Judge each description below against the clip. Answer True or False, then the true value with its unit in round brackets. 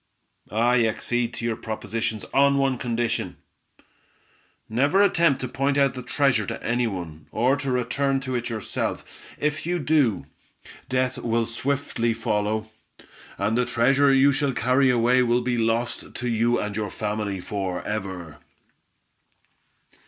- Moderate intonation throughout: True (3.6 semitones)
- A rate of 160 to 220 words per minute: False (145 wpm)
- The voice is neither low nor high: False (120 Hz)